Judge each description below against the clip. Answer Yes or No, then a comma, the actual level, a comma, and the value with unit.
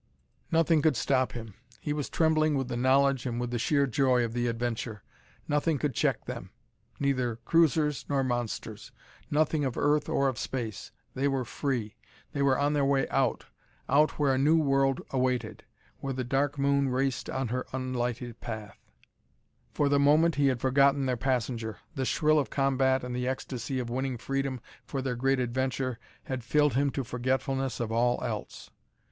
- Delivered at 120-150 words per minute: No, average, 175 wpm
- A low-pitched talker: Yes, low, 130 Hz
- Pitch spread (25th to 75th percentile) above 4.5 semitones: No, narrow, 2.4 semitones